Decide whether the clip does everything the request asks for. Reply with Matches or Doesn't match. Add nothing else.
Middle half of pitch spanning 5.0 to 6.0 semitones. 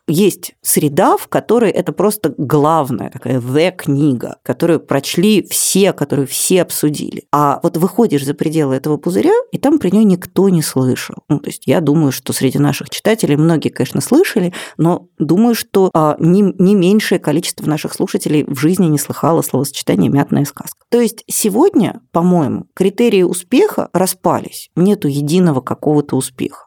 Matches